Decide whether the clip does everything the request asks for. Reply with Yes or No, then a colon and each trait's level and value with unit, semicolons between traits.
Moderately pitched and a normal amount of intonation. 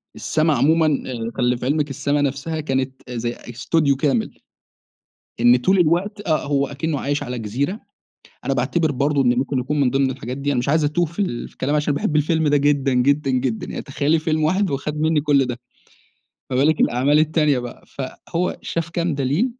Yes: medium, 145 Hz; average, 3.1 semitones